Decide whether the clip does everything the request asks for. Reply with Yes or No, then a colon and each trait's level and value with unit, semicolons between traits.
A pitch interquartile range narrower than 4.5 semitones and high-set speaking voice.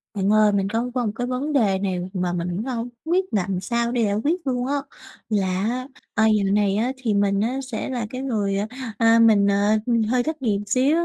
Yes: average, 3.9 semitones; high, 220 Hz